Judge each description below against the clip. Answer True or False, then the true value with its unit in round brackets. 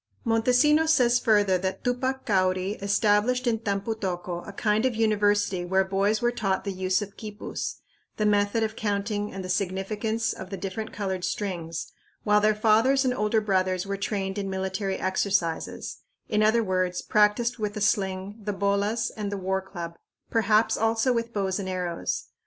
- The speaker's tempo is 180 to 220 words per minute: False (170 wpm)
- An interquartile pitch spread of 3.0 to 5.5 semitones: False (2.6 semitones)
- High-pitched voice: True (205 Hz)